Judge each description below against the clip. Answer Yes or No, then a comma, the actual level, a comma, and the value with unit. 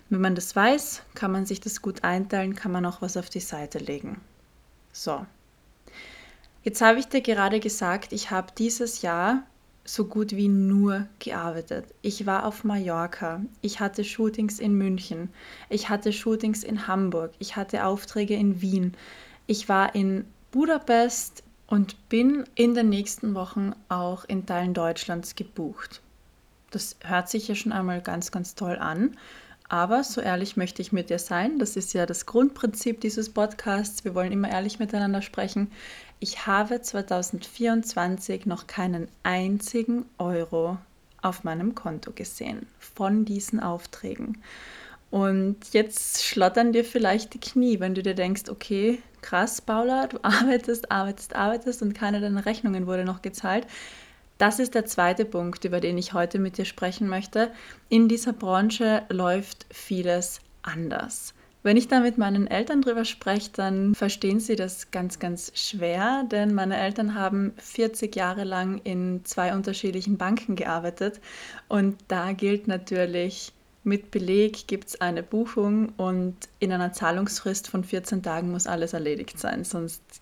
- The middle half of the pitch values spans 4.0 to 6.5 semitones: No, average, 3.3 semitones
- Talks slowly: No, average, 155 wpm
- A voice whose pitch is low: No, high, 200 Hz